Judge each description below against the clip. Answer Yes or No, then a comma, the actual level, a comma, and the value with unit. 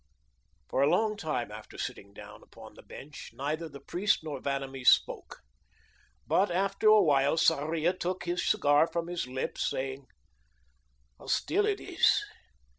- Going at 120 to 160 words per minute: Yes, average, 150 wpm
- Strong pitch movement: No, average, 4.8 semitones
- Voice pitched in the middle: Yes, medium, 160 Hz